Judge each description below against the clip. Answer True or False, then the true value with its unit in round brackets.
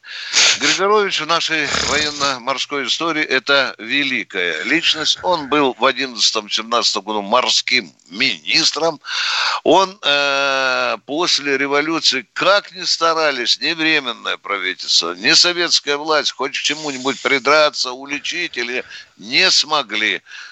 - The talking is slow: True (105 wpm)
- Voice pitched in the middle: True (145 Hz)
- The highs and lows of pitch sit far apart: False (3.5 semitones)